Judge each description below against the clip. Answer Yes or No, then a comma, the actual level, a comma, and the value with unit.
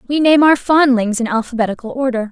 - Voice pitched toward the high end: Yes, very high, 255 Hz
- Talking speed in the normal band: Yes, average, 180 wpm